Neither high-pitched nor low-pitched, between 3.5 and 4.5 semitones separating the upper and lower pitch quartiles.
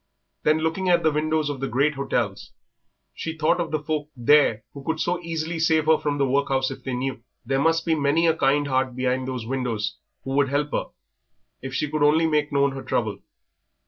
No: medium, 145 Hz; average, 3.0 semitones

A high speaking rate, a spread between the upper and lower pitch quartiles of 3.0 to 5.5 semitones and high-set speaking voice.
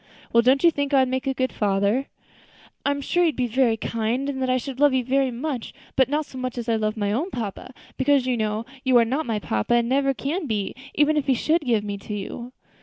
Yes: fast, 260 wpm; average, 3.4 semitones; very high, 255 Hz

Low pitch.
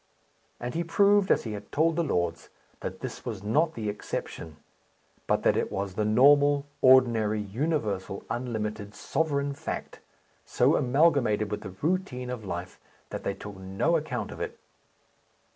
Yes: low, 120 Hz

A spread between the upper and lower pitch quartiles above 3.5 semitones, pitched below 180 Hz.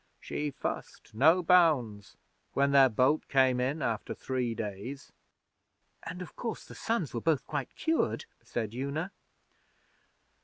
Yes: average, 5.0 semitones; medium, 140 Hz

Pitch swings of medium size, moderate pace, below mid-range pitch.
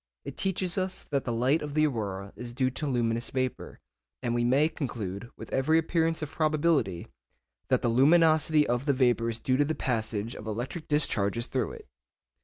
Yes: average, 4.7 semitones; average, 190 wpm; low, 130 Hz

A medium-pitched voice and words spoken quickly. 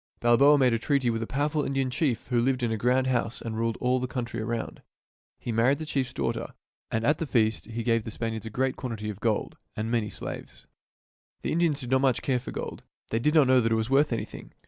No: low, 125 Hz; fast, 255 wpm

